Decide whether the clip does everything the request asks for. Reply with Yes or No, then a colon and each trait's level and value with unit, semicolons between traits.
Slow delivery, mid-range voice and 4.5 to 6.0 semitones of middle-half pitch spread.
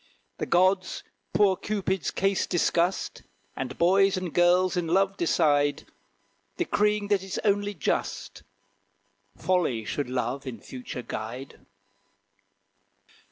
Yes: slow, 110 wpm; medium, 180 Hz; average, 5.2 semitones